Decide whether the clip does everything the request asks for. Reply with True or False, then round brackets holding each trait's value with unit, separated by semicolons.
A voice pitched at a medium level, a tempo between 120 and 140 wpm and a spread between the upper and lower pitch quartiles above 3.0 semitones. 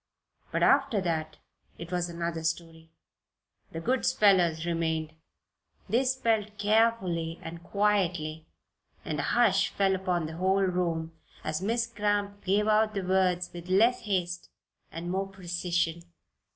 True (180 Hz; 135 wpm; 3.6 semitones)